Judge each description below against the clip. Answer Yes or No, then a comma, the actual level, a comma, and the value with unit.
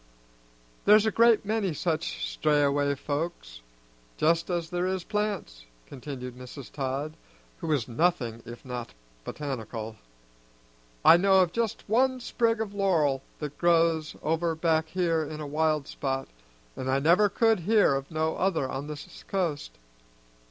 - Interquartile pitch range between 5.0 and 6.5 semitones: Yes, wide, 5.5 semitones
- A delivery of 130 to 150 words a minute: Yes, average, 145 wpm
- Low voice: No, medium, 160 Hz